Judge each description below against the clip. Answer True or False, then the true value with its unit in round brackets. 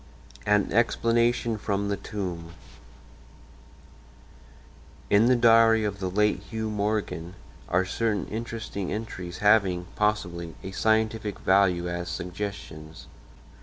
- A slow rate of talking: True (110 wpm)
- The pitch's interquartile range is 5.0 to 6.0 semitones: False (3.5 semitones)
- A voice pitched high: False (105 Hz)